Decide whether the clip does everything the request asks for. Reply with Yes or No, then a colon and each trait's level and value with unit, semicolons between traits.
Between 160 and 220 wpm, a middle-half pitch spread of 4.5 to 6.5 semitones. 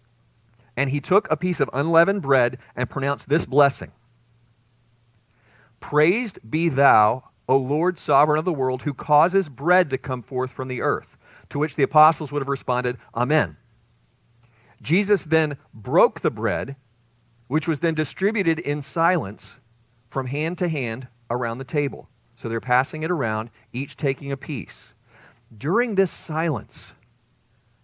No: average, 145 wpm; average, 4.8 semitones